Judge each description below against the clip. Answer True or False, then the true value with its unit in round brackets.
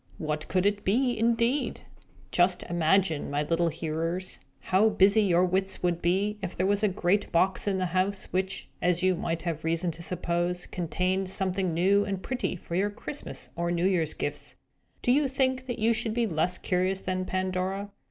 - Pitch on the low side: False (185 Hz)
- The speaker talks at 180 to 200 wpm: True (185 wpm)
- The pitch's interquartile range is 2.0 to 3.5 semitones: True (2.8 semitones)